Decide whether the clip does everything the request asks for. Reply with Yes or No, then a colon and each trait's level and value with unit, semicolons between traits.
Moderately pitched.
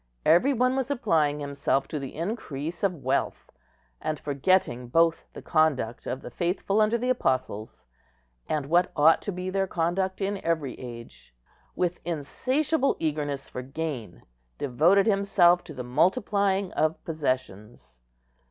Yes: medium, 165 Hz